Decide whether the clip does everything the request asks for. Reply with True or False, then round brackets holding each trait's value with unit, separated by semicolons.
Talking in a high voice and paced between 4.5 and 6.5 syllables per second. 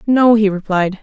True (210 Hz; 4.6 syllables/s)